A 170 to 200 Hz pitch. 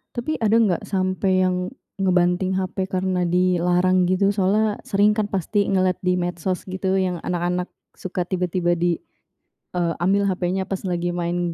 Yes: medium, 185 Hz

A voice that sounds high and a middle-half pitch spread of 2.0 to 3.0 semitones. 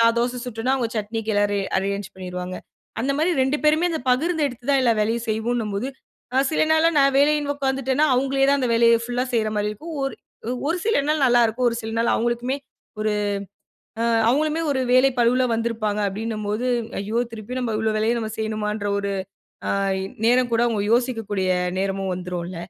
No: high, 235 Hz; average, 3.9 semitones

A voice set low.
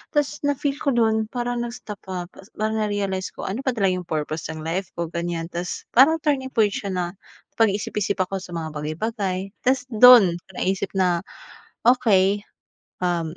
No: high, 195 Hz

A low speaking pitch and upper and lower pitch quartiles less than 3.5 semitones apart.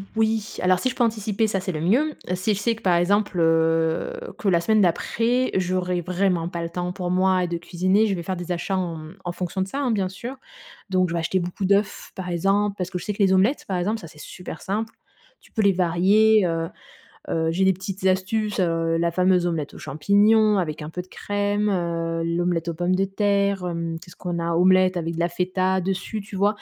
No: medium, 185 Hz; average, 2.9 semitones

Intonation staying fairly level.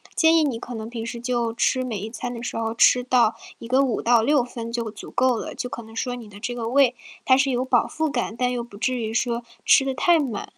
Yes: narrow, 2.1 semitones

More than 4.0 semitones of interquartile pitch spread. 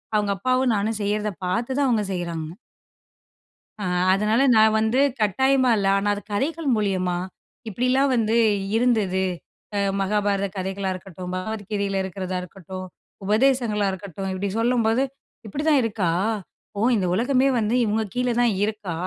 No: average, 3.7 semitones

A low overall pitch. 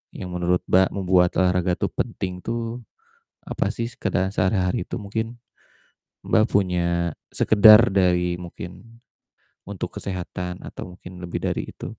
Yes: very low, 90 Hz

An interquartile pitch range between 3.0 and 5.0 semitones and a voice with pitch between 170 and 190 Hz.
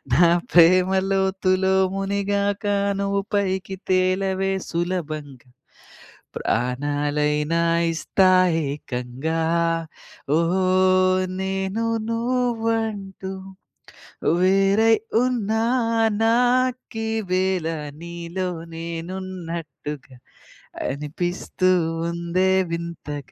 Yes: average, 3.3 semitones; medium, 185 Hz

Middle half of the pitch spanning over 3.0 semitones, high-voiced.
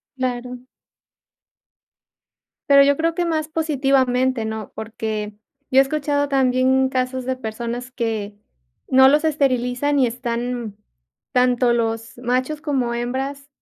No: narrow, 2.6 semitones; very high, 255 Hz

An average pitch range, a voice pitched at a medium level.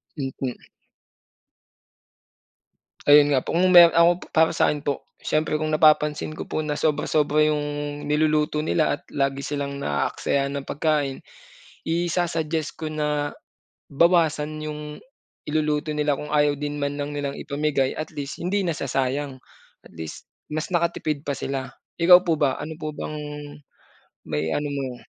No: narrow, 1.7 semitones; medium, 150 Hz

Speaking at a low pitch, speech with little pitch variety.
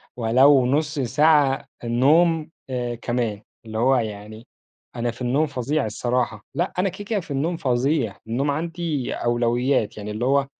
No: low, 130 Hz; average, 4.1 semitones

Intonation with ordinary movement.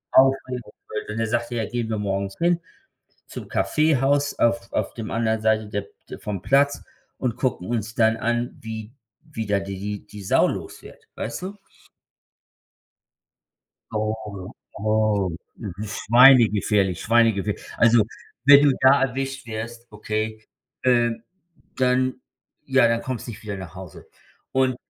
Yes: average, 3.4 semitones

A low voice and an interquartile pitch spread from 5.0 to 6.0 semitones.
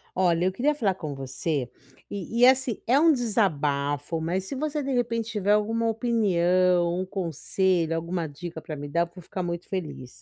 No: medium, 185 Hz; wide, 5.6 semitones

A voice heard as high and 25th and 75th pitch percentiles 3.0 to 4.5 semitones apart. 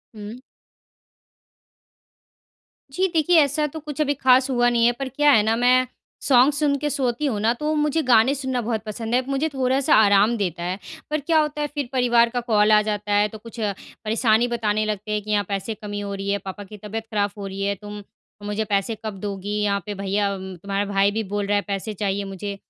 Yes: high, 220 Hz; average, 4.2 semitones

